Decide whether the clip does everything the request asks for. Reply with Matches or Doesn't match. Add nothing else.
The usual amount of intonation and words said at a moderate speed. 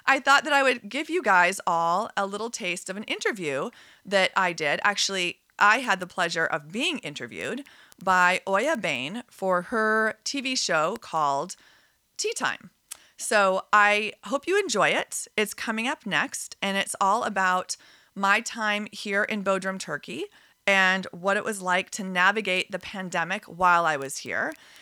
Matches